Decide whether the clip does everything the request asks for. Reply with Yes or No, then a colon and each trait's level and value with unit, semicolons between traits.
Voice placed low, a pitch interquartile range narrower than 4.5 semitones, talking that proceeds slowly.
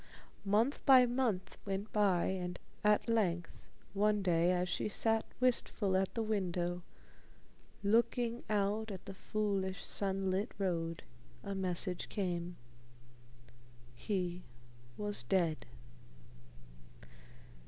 No: high, 195 Hz; average, 3.0 semitones; slow, 100 wpm